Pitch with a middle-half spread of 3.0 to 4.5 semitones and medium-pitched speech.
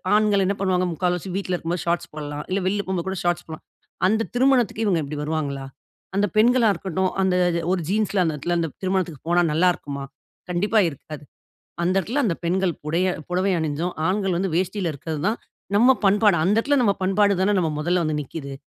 Yes: average, 3.6 semitones; medium, 180 Hz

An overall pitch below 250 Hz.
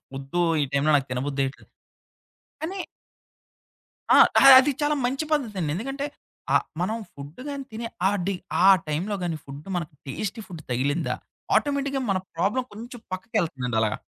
Yes: medium, 185 Hz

